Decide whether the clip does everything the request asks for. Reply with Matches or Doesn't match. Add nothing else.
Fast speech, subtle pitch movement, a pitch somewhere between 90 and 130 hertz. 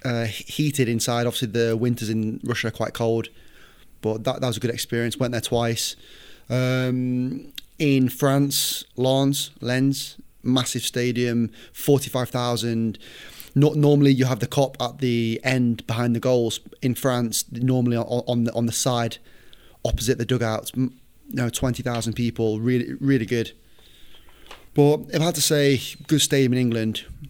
Matches